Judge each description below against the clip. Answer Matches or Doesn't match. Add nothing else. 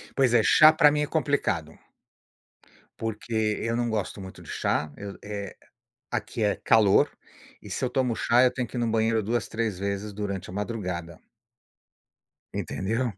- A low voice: Matches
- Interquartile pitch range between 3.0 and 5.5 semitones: Matches